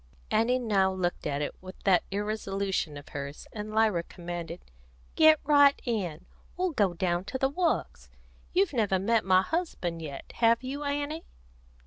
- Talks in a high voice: Yes, high, 205 Hz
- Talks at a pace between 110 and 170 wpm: Yes, average, 155 wpm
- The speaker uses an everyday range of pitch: No, wide, 7.3 semitones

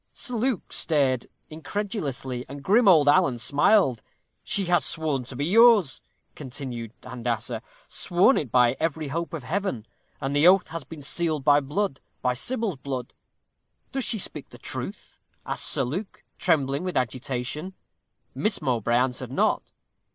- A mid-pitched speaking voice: Yes, medium, 145 Hz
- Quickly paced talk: No, average, 150 wpm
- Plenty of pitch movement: Yes, wide, 6.1 semitones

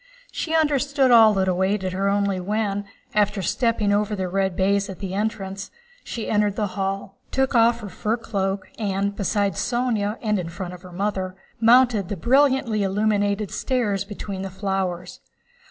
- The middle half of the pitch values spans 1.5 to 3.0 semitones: Yes, narrow, 2.4 semitones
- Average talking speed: Yes, average, 165 wpm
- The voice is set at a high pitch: Yes, high, 205 Hz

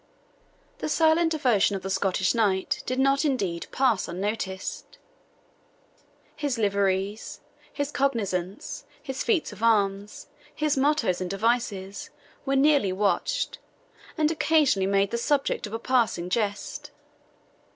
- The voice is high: Yes, high, 225 Hz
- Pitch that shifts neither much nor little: No, wide, 6.0 semitones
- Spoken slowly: Yes, slow, 120 wpm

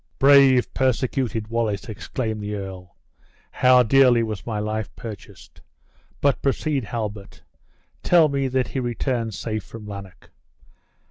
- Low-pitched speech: Yes, low, 115 Hz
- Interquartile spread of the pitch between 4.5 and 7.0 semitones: No, average, 3.7 semitones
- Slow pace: Yes, slow, 125 wpm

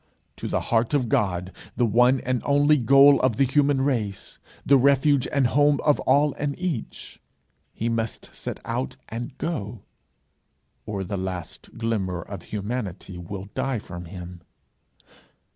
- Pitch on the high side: No, low, 120 Hz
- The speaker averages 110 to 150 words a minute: Yes, average, 145 wpm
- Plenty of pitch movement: Yes, wide, 5.9 semitones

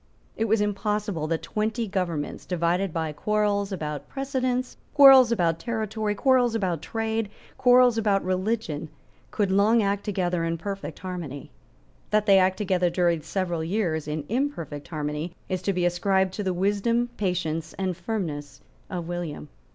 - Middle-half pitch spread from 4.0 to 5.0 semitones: Yes, average, 4.3 semitones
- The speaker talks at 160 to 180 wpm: No, average, 150 wpm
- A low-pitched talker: No, high, 190 Hz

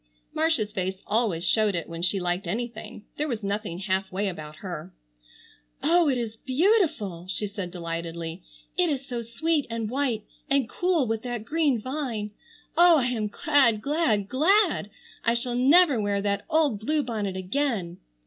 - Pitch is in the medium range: No, high, 225 Hz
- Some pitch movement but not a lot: No, wide, 6.6 semitones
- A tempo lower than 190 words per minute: Yes, average, 165 wpm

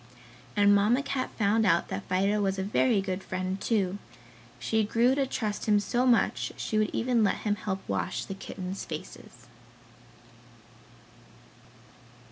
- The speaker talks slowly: No, average, 145 wpm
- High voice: Yes, high, 205 Hz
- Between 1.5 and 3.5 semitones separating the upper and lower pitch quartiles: Yes, average, 2.9 semitones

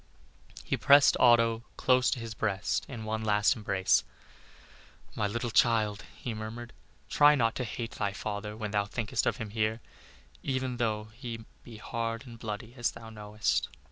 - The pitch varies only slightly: Yes, narrow, 2.0 semitones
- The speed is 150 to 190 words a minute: Yes, average, 165 wpm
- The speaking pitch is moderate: No, low, 115 Hz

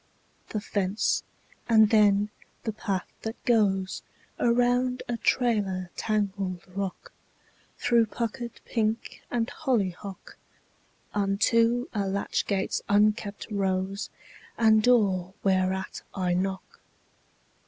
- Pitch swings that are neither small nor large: Yes, average, 3.0 semitones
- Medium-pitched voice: No, high, 205 Hz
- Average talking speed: No, slow, 100 wpm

